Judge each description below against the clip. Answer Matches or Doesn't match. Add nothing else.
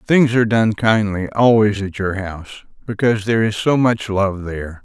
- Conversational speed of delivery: Matches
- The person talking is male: Matches